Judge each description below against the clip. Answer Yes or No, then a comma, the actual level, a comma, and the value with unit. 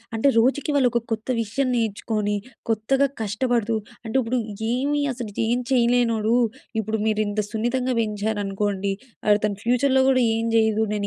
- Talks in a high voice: Yes, high, 225 Hz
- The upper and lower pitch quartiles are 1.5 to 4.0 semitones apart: Yes, average, 2.7 semitones